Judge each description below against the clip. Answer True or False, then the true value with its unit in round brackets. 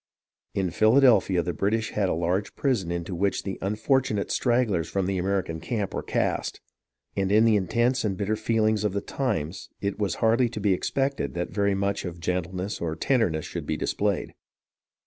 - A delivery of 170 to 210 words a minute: True (180 wpm)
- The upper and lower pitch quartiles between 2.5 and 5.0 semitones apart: True (3.5 semitones)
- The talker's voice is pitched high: False (100 Hz)